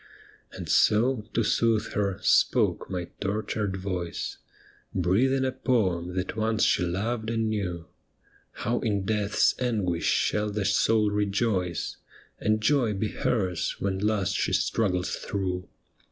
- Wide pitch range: No, average, 3.0 semitones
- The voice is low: Yes, low, 105 Hz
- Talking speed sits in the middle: No, slow, 130 wpm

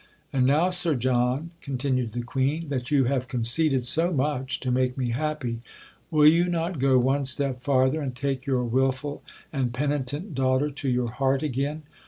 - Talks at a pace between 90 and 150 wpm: No, average, 175 wpm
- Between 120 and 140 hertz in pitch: Yes, low, 135 Hz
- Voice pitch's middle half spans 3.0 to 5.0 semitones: No, narrow, 2.6 semitones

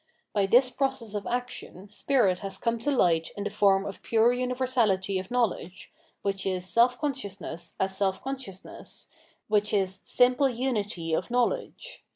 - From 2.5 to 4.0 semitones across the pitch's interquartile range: No, average, 4.5 semitones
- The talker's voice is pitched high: Yes, high, 210 Hz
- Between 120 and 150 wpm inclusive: No, average, 160 wpm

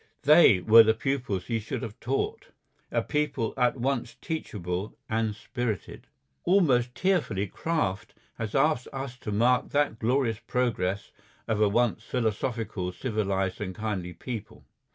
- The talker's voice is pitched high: No, low, 115 Hz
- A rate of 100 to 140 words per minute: Yes, slow, 135 wpm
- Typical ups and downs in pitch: Yes, average, 4.0 semitones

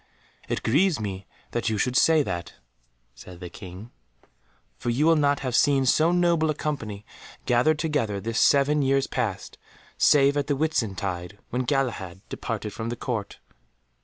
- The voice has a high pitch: No, low, 125 Hz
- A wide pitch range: Yes, wide, 6.1 semitones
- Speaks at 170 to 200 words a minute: No, average, 155 wpm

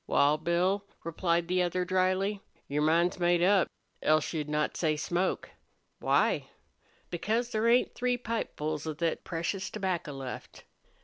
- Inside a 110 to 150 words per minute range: Yes, average, 140 wpm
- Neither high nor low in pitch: Yes, medium, 175 Hz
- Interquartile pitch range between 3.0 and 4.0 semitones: Yes, average, 3.6 semitones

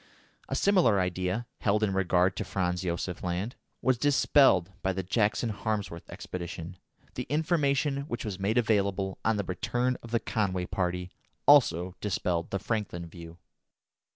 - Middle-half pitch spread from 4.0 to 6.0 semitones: Yes, average, 4.7 semitones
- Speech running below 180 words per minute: Yes, average, 150 wpm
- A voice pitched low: Yes, low, 100 Hz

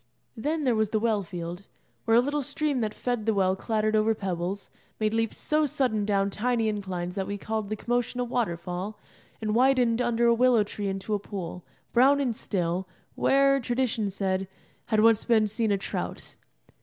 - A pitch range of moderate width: Yes, average, 3.6 semitones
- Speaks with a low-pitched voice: No, high, 220 Hz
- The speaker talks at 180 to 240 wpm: Yes, average, 185 wpm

